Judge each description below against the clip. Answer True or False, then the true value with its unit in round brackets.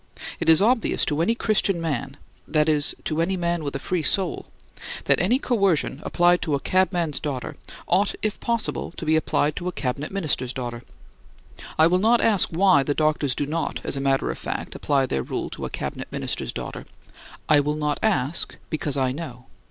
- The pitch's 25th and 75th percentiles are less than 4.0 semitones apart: False (4.4 semitones)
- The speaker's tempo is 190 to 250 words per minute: True (195 wpm)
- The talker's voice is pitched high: False (160 Hz)